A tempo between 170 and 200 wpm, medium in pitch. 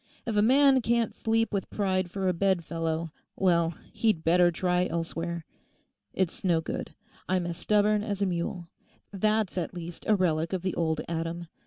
Yes: average, 175 wpm; medium, 180 Hz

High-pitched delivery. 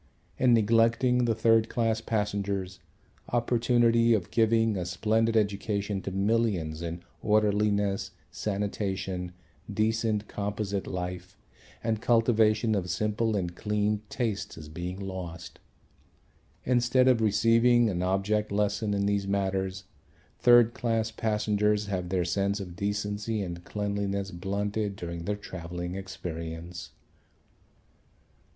No: low, 105 Hz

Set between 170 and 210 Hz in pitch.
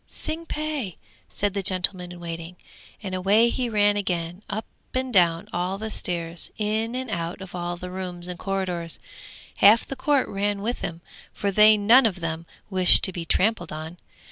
Yes: high, 190 Hz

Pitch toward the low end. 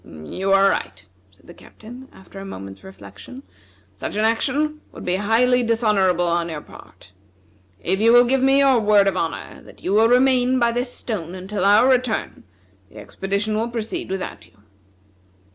No: high, 215 Hz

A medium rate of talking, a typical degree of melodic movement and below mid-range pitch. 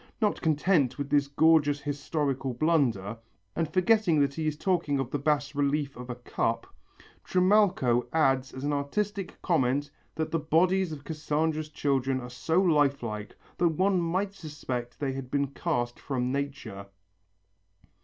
No: average, 155 wpm; average, 3.5 semitones; medium, 145 Hz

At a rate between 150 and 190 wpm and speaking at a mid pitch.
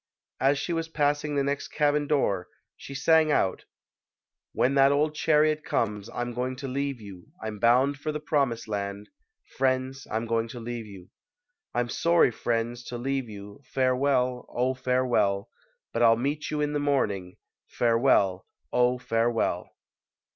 No: average, 155 wpm; low, 125 Hz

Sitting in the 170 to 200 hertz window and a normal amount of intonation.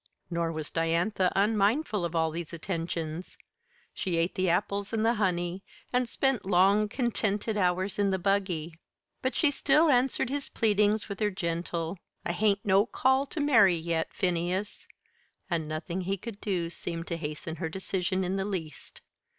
Yes: high, 190 Hz; average, 3.7 semitones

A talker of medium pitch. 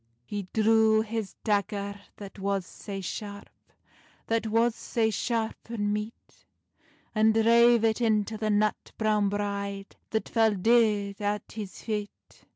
No: high, 215 Hz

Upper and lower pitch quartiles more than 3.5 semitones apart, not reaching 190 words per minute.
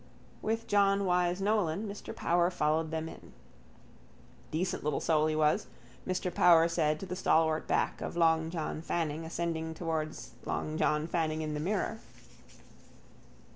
No: narrow, 2.4 semitones; average, 145 wpm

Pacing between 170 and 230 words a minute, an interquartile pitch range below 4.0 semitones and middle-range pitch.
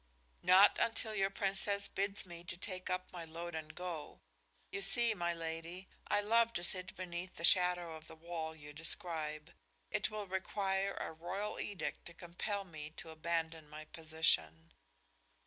No: average, 160 wpm; average, 3.2 semitones; medium, 175 Hz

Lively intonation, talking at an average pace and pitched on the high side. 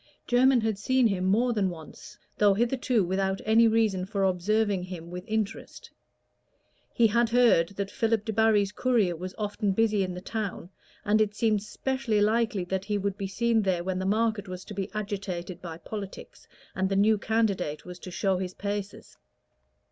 No: average, 2.8 semitones; average, 180 wpm; high, 205 Hz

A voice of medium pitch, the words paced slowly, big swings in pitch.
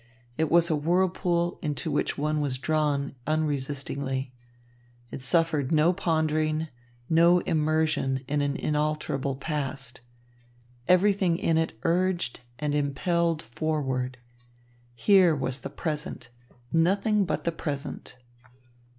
No: medium, 155 Hz; slow, 110 wpm; average, 3.2 semitones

